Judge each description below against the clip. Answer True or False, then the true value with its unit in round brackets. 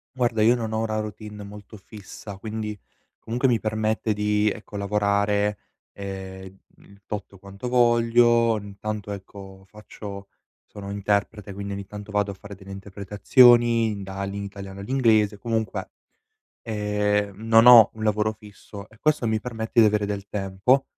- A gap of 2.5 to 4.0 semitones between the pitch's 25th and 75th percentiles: False (1.9 semitones)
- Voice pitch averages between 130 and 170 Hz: False (105 Hz)